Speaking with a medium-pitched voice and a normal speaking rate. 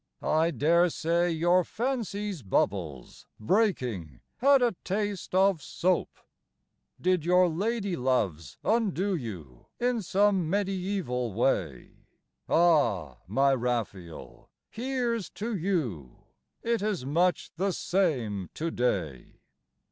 No: medium, 170 Hz; slow, 105 wpm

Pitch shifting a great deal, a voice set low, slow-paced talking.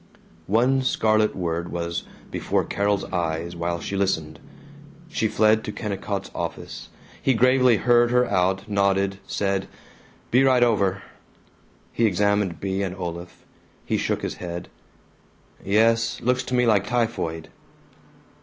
No: average, 4.2 semitones; low, 100 Hz; slow, 130 wpm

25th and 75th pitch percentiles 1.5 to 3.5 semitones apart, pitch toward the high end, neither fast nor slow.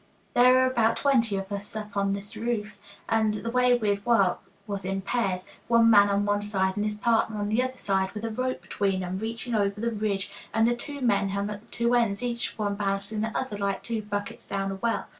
No: average, 2.7 semitones; high, 210 Hz; fast, 230 wpm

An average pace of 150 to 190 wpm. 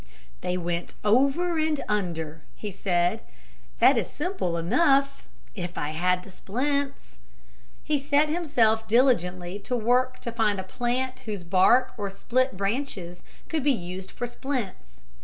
No: average, 140 wpm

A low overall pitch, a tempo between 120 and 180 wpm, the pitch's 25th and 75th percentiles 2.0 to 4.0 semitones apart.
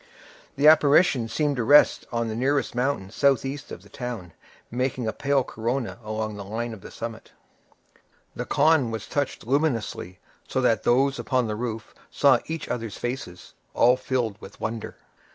Yes: low, 125 Hz; average, 165 wpm; average, 3.7 semitones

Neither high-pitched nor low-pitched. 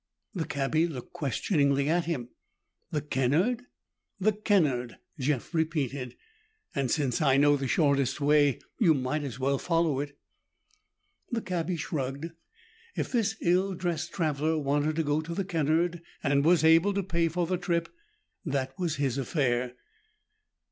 Yes: medium, 155 Hz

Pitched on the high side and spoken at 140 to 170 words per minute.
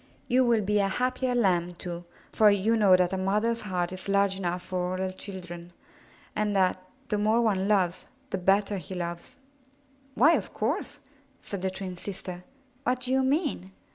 No: high, 195 Hz; average, 180 wpm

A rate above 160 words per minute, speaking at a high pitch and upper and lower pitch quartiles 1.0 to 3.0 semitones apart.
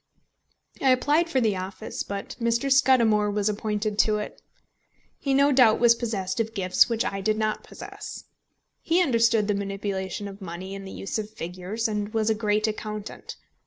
Yes: average, 175 wpm; high, 215 Hz; narrow, 2.6 semitones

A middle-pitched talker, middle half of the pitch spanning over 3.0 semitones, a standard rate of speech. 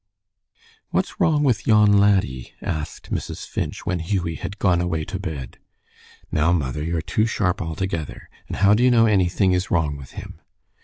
No: very low, 90 Hz; average, 4.3 semitones; average, 170 wpm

